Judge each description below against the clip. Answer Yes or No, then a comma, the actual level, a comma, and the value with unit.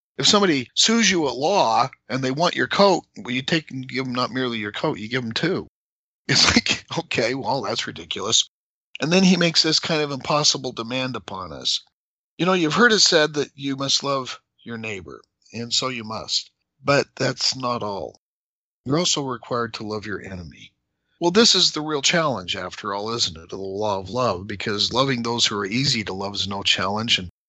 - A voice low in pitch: Yes, low, 130 Hz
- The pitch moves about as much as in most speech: No, wide, 6.2 semitones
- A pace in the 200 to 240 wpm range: Yes, fast, 205 wpm